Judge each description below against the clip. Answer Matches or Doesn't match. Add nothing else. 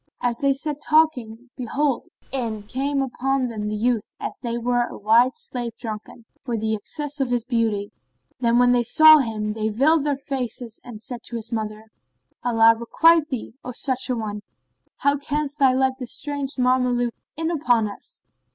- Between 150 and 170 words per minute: Doesn't match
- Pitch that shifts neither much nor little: Matches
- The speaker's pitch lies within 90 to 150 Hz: Doesn't match